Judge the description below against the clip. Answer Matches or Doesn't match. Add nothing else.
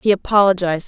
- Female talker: Matches